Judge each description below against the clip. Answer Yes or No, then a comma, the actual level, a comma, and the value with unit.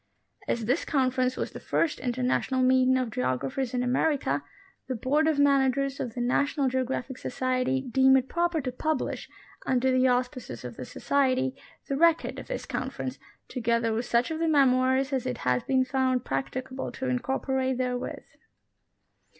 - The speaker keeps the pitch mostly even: Yes, narrow, 1.4 semitones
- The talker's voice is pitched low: No, very high, 260 Hz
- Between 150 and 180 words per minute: Yes, average, 160 wpm